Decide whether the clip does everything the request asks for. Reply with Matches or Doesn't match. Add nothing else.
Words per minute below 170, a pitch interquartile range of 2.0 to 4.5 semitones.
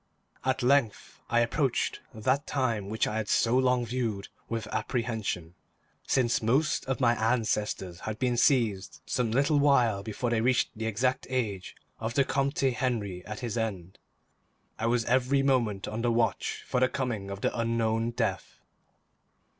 Matches